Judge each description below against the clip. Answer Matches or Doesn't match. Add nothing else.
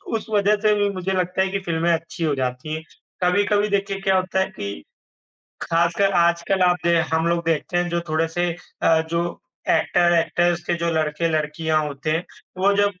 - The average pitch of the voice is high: Doesn't match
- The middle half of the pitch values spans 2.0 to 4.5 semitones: Matches